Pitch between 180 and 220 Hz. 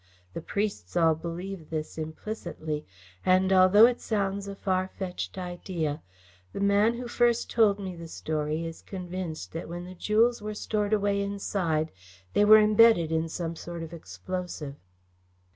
Yes: medium, 185 Hz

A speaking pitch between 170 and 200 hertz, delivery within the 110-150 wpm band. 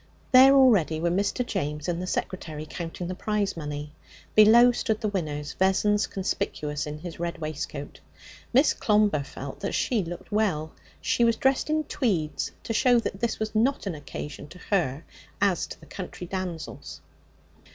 No: medium, 185 Hz; average, 165 wpm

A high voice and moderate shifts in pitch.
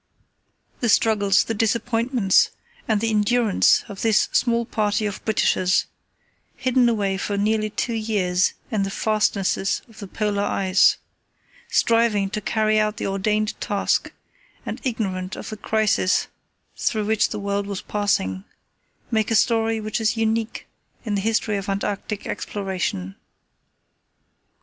No: high, 210 Hz; narrow, 2.0 semitones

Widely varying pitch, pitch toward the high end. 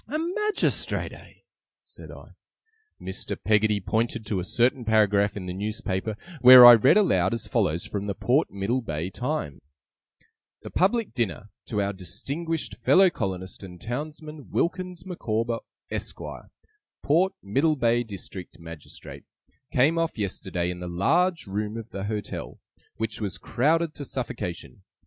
No: wide, 7.2 semitones; low, 110 Hz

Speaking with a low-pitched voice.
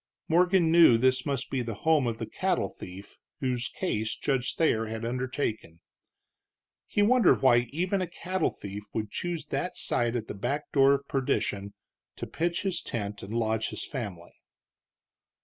Yes: low, 125 Hz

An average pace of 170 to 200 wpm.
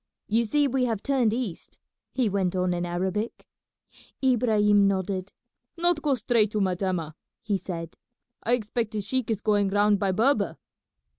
No: average, 155 wpm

